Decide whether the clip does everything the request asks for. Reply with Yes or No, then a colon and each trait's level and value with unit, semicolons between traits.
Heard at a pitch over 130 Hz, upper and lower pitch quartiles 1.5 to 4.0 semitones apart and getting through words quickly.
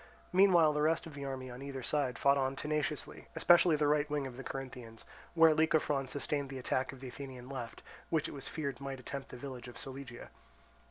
Yes: medium, 140 Hz; narrow, 2.5 semitones; fast, 210 wpm